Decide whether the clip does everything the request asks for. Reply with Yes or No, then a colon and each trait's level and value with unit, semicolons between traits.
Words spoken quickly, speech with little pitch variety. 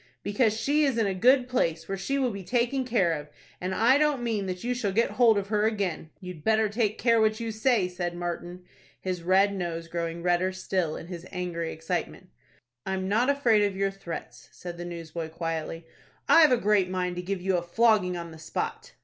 No: fast, 210 wpm; average, 4.3 semitones